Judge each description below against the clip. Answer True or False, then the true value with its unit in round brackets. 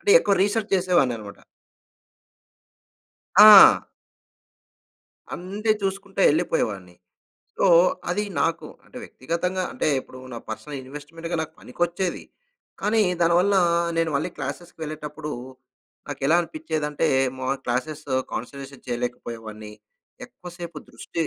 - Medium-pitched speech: True (160 Hz)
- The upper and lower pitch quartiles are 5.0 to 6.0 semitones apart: True (5.5 semitones)